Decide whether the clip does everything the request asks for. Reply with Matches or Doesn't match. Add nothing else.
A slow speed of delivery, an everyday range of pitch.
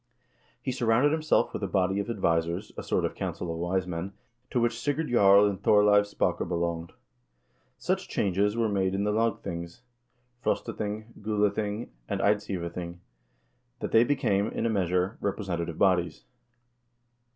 Doesn't match